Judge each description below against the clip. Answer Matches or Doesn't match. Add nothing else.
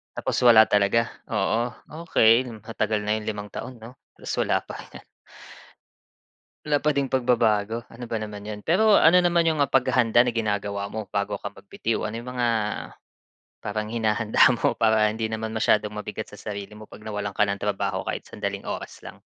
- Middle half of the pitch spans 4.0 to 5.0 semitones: Doesn't match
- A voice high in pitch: Doesn't match